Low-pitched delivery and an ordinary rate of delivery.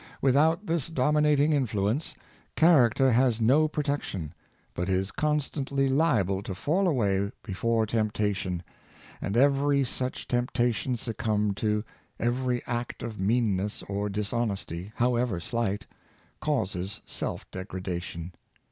No: low, 115 Hz; slow, 115 wpm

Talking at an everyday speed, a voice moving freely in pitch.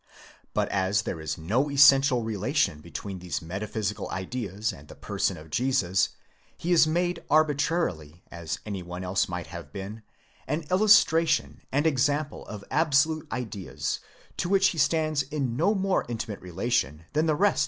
Yes: average, 165 wpm; wide, 8.7 semitones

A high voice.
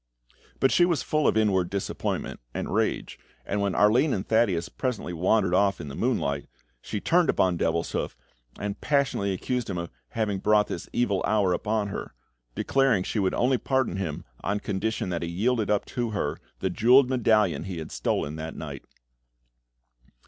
No: low, 105 Hz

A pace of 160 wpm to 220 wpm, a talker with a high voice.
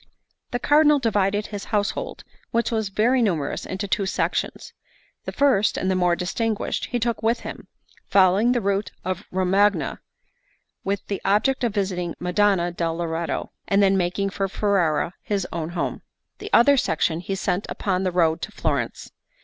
Yes: average, 165 wpm; high, 195 Hz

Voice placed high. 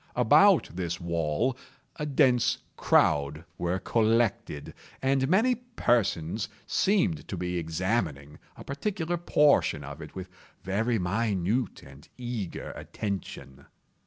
No: low, 100 Hz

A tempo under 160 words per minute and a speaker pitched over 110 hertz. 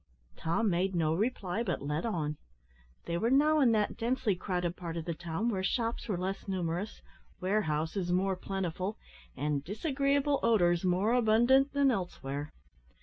Yes: average, 150 wpm; high, 190 Hz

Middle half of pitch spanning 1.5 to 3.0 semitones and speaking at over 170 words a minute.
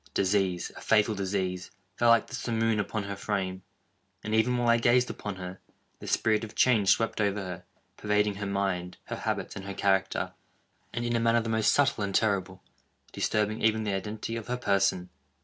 Yes: average, 2.7 semitones; average, 185 wpm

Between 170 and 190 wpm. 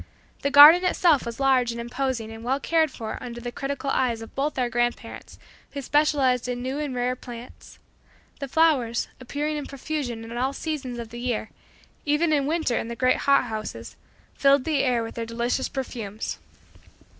Yes: average, 185 wpm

